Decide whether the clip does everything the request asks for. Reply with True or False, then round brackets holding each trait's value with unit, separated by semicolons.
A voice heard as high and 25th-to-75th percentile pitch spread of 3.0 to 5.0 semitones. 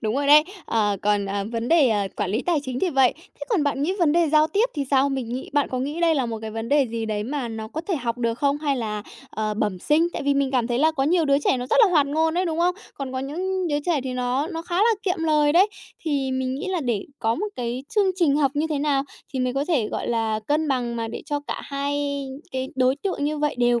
True (280 Hz; 4.6 semitones)